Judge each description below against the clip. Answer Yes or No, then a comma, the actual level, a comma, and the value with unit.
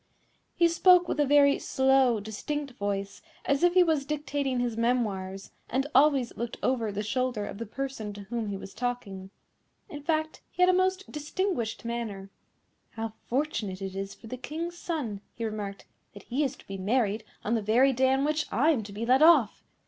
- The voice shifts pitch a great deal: Yes, wide, 5.7 semitones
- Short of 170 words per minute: No, average, 195 wpm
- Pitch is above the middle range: Yes, high, 245 Hz